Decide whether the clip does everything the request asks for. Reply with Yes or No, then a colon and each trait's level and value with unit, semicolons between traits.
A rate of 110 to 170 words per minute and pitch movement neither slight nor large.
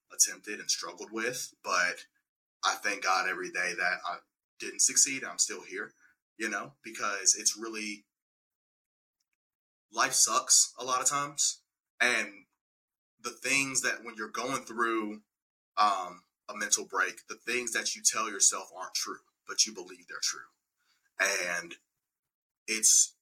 Yes: average, 140 wpm; average, 3.0 semitones